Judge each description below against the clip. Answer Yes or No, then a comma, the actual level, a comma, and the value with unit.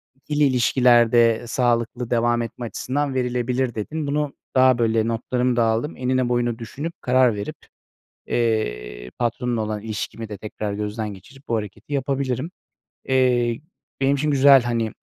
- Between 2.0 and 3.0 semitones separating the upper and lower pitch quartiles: Yes, narrow, 2.5 semitones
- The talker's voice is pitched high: No, low, 120 Hz